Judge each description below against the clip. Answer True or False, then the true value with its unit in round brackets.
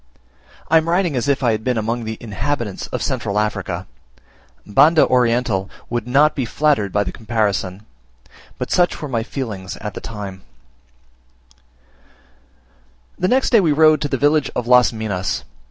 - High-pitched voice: False (120 Hz)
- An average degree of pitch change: False (5.8 semitones)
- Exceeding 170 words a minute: False (160 wpm)